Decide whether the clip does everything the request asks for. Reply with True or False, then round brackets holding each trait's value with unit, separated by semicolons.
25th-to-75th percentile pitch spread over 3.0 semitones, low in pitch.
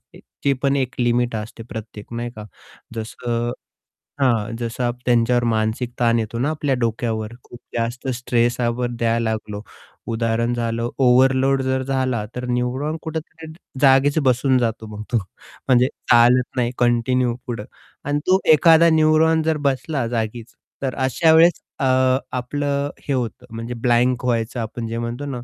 False (2.4 semitones; 125 Hz)